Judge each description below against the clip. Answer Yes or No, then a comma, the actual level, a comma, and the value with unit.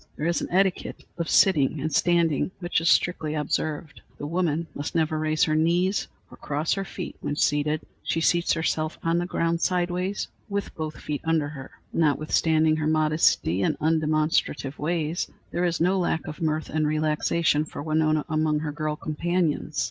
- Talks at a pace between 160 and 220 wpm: Yes, average, 170 wpm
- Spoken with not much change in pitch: Yes, narrow, 1.9 semitones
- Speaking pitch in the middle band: Yes, medium, 155 Hz